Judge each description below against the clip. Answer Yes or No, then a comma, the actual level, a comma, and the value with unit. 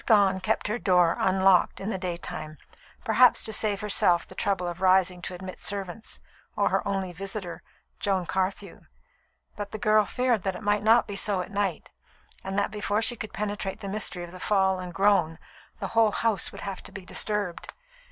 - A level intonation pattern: Yes, narrow, 2.3 semitones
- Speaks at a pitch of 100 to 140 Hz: No, high, 195 Hz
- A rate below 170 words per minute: No, average, 195 wpm